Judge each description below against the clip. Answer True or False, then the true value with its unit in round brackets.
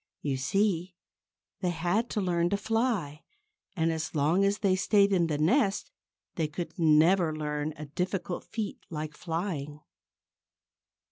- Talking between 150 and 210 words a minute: False (140 wpm)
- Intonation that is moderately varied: True (4.3 semitones)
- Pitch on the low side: False (175 Hz)